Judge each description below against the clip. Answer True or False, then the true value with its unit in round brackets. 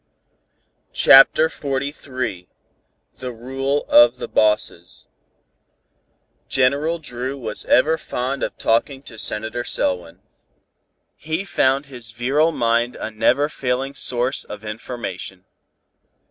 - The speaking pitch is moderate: False (125 Hz)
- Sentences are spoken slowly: True (105 wpm)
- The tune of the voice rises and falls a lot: False (3.6 semitones)